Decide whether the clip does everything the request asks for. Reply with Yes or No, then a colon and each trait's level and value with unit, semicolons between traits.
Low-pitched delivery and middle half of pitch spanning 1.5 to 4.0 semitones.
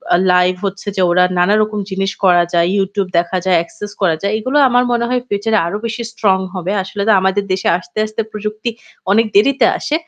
No: high, 200 Hz; average, 2.8 semitones